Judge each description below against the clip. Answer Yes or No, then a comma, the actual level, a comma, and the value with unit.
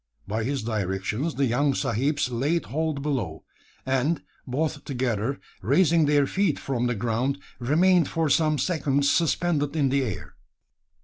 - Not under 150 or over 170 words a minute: No, average, 140 wpm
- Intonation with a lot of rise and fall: No, average, 4.1 semitones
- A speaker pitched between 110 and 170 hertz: Yes, medium, 140 Hz